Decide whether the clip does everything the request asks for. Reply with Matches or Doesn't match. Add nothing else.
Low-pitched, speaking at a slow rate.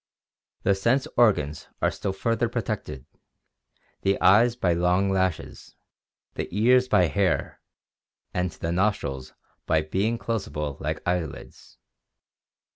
Matches